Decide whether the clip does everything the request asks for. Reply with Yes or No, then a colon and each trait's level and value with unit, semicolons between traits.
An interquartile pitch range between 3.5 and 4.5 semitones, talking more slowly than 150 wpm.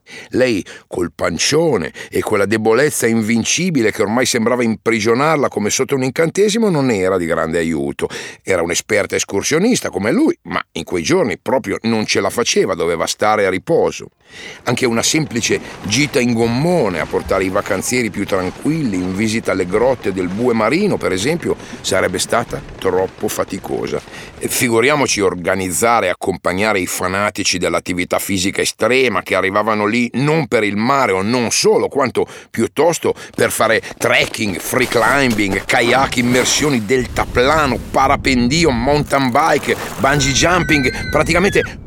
No: average, 5.2 semitones; average, 140 wpm